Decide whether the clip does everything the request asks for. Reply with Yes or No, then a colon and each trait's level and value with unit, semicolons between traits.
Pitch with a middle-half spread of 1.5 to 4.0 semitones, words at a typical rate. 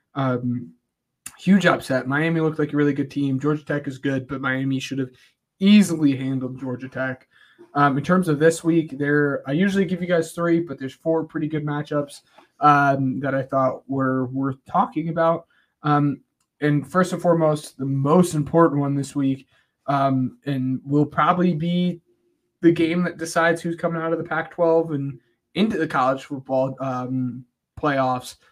Yes: average, 3.7 semitones; average, 175 wpm